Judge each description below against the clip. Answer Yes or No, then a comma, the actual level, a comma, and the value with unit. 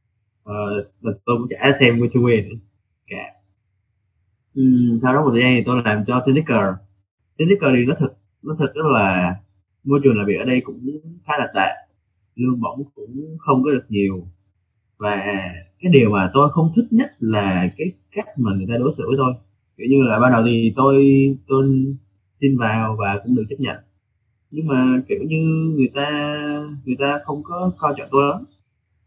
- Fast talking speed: No, average, 190 wpm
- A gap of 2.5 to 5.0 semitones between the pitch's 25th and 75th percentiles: No, wide, 5.4 semitones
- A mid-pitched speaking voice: No, low, 125 Hz